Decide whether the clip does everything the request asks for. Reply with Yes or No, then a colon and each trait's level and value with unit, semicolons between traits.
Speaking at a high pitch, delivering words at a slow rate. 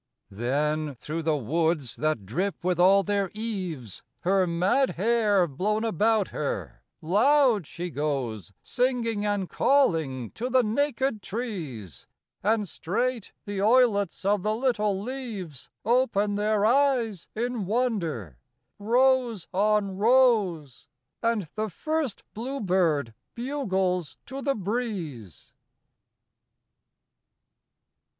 Yes: high, 205 Hz; slow, 105 wpm